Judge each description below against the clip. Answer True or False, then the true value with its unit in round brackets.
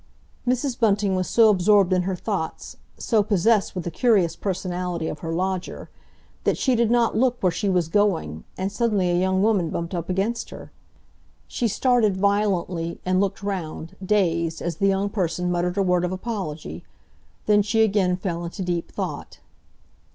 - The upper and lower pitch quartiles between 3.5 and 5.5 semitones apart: False (3.0 semitones)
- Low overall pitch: False (190 Hz)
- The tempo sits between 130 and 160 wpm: False (170 wpm)